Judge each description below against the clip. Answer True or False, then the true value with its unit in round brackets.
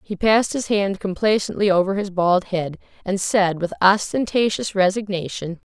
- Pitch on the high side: True (195 Hz)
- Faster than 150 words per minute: False (145 wpm)